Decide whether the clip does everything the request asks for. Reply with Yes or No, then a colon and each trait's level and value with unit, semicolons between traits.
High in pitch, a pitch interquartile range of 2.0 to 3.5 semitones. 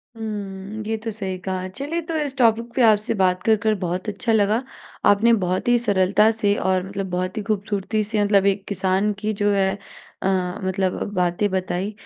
Yes: high, 200 Hz; narrow, 2.5 semitones